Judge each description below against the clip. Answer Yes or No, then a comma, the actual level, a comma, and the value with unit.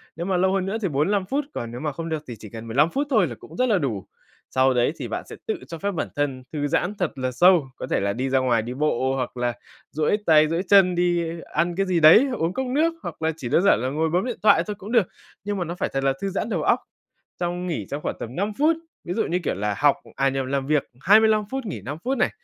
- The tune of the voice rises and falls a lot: Yes, wide, 6.5 semitones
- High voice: No, medium, 165 Hz